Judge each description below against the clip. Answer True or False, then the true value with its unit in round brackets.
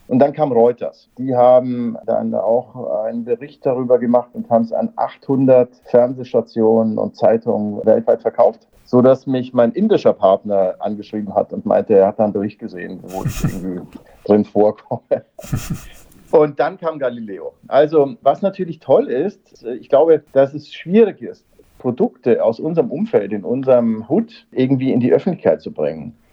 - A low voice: True (125 Hz)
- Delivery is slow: False (160 wpm)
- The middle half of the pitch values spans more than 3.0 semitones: True (3.8 semitones)